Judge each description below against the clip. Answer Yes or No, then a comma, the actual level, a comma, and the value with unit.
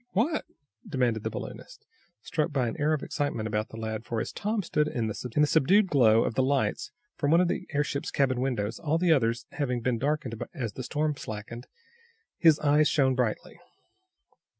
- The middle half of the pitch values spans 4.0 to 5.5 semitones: Yes, average, 4.7 semitones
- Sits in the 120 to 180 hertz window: Yes, low, 135 Hz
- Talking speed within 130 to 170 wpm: No, average, 185 wpm